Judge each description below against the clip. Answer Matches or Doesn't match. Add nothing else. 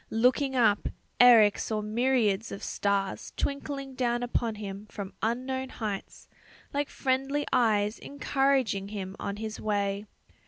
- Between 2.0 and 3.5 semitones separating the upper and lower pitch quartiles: Doesn't match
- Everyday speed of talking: Doesn't match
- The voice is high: Matches